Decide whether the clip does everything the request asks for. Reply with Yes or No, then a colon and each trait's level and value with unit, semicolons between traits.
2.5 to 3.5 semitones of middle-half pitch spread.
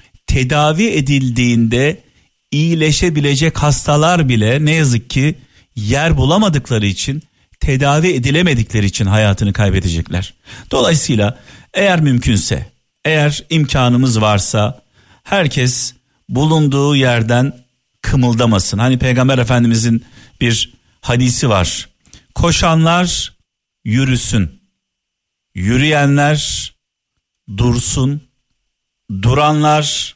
No: average, 4.8 semitones